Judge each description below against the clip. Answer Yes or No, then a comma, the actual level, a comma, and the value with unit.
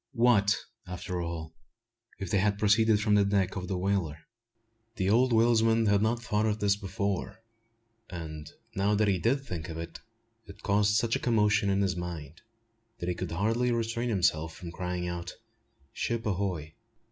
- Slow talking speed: No, average, 170 wpm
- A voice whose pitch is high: No, low, 100 Hz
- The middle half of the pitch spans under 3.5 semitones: No, average, 3.8 semitones